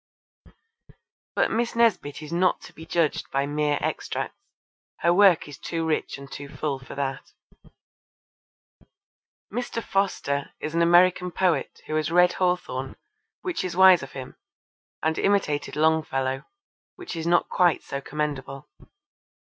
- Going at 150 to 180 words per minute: No, average, 140 wpm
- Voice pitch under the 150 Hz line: No, medium, 160 Hz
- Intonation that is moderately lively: Yes, average, 4.2 semitones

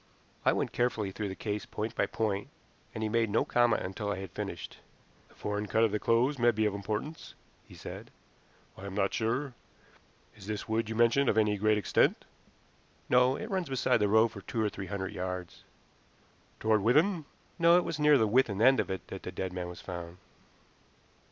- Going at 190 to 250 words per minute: Yes, fast, 205 wpm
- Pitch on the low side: Yes, low, 110 Hz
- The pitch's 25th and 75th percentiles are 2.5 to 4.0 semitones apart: Yes, average, 3.5 semitones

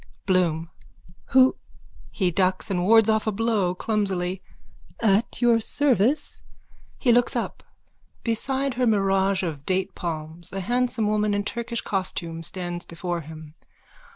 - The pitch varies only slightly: No, average, 4.3 semitones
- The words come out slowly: Yes, slow, 125 wpm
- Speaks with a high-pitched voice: Yes, high, 195 Hz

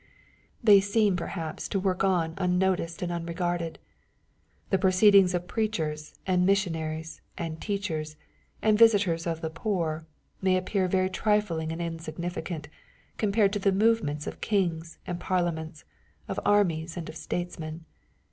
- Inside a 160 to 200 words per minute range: No, slow, 135 wpm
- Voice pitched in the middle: Yes, medium, 175 Hz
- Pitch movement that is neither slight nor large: Yes, average, 3.2 semitones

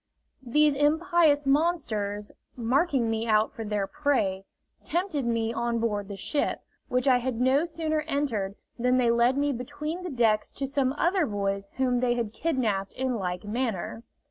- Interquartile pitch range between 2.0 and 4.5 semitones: No, average, 5.0 semitones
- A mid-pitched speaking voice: No, very high, 250 Hz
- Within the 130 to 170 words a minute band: Yes, average, 165 wpm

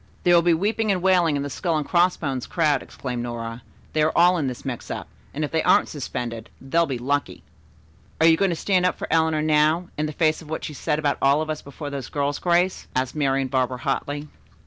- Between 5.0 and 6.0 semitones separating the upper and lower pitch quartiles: No, average, 3.8 semitones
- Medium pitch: Yes, medium, 150 Hz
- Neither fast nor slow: No, fast, 235 wpm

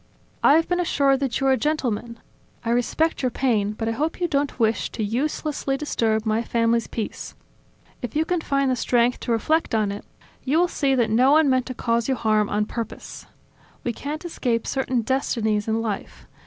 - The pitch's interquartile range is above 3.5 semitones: Yes, average, 4.0 semitones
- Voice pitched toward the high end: Yes, high, 245 Hz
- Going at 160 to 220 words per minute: Yes, average, 200 wpm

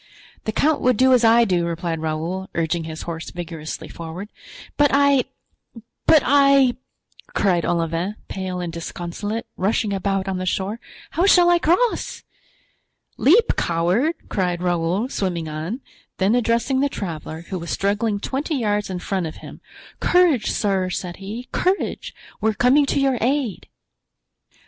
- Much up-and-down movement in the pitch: Yes, wide, 6.9 semitones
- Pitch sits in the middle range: No, high, 200 Hz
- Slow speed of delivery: No, average, 150 wpm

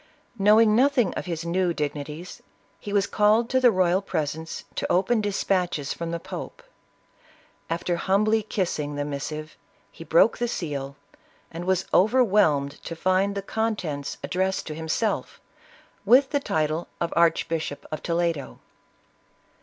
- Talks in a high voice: No, medium, 180 Hz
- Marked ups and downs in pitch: No, average, 4.8 semitones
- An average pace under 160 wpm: Yes, average, 145 wpm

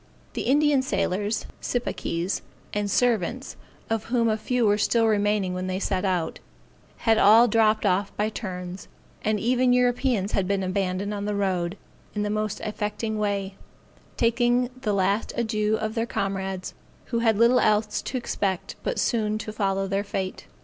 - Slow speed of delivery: No, average, 165 wpm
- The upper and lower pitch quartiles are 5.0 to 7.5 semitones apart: No, average, 2.8 semitones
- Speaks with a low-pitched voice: No, high, 210 Hz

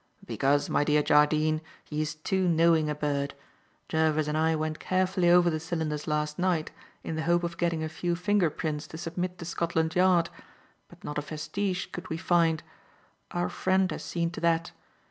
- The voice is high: No, medium, 160 Hz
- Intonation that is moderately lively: No, narrow, 2.2 semitones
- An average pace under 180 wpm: No, average, 185 wpm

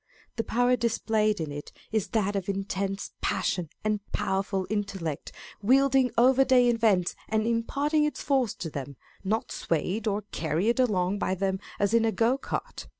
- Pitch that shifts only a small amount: No, average, 3.6 semitones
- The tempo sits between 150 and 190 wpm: Yes, average, 165 wpm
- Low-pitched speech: No, high, 215 Hz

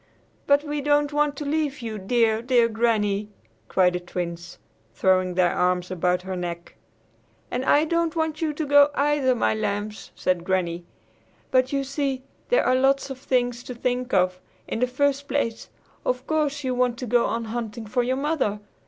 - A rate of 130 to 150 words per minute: No, average, 180 wpm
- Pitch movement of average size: No, wide, 6.0 semitones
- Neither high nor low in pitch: No, high, 245 Hz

